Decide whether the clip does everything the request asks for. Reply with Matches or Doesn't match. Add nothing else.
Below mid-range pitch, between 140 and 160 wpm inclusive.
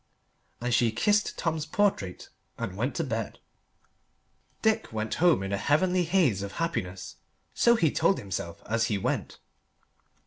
Matches